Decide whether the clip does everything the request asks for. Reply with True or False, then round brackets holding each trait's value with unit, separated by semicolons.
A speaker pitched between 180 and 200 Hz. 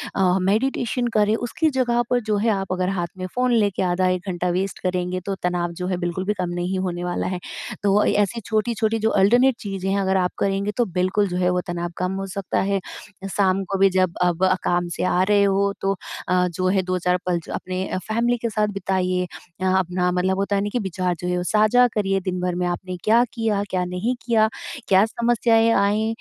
True (190 Hz)